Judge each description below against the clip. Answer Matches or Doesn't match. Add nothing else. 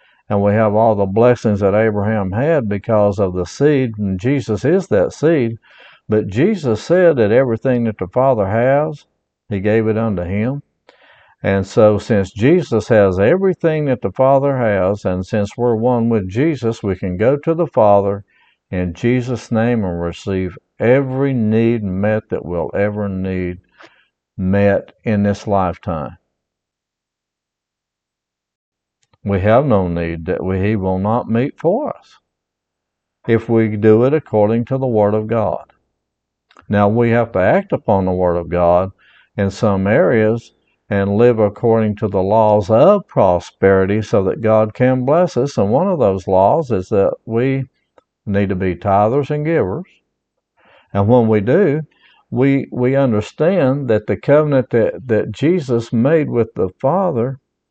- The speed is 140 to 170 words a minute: Matches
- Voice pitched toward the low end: Matches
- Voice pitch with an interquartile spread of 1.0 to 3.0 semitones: Doesn't match